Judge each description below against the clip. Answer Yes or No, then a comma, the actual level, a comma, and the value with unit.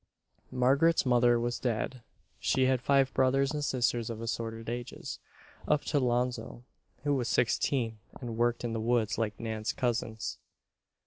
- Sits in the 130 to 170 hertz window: No, low, 120 Hz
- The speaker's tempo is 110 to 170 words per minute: Yes, average, 145 wpm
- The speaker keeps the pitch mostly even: Yes, narrow, 2.3 semitones